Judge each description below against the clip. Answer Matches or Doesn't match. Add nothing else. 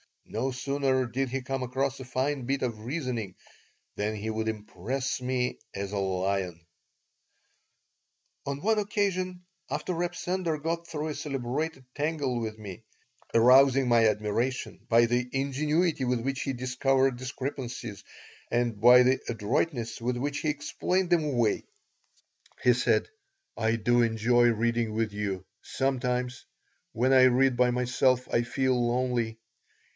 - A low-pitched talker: Matches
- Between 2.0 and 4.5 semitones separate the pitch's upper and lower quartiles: Matches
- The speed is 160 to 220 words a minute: Doesn't match